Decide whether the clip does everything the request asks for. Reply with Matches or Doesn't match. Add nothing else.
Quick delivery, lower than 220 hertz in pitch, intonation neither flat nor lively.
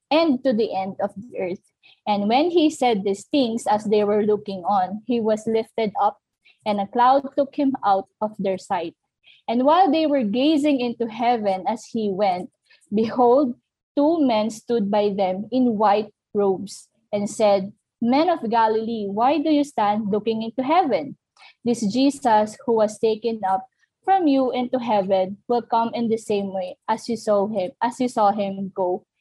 Doesn't match